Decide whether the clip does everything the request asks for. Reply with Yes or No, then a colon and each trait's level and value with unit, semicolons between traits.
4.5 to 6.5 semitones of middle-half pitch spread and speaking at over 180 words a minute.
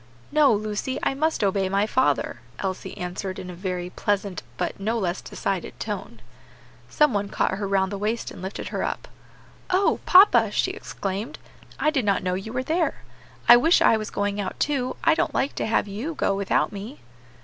Yes: average, 5.1 semitones; average, 190 wpm